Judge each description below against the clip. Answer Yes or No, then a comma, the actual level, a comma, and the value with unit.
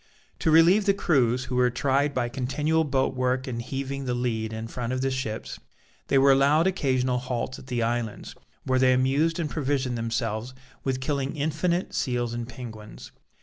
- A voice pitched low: Yes, low, 130 Hz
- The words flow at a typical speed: Yes, average, 180 wpm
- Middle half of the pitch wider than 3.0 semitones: No, narrow, 2.6 semitones